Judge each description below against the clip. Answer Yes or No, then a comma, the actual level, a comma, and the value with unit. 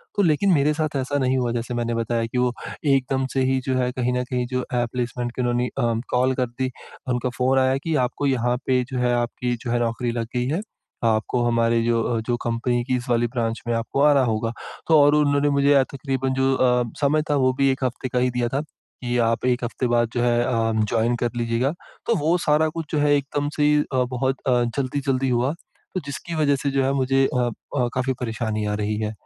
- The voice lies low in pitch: Yes, low, 125 Hz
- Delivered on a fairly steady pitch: Yes, narrow, 2.3 semitones